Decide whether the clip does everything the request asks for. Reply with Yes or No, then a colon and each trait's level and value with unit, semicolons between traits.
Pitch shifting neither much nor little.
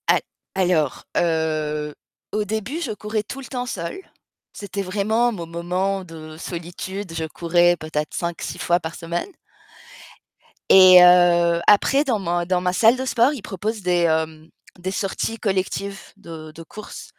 Yes: average, 3.8 semitones